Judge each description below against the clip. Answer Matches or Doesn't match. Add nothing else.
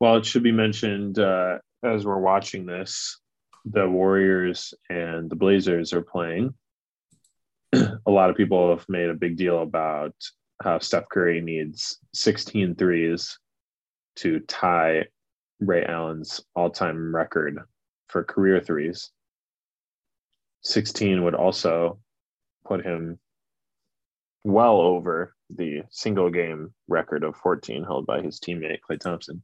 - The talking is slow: Matches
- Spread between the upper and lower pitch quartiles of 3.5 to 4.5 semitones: Doesn't match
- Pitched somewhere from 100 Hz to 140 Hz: Doesn't match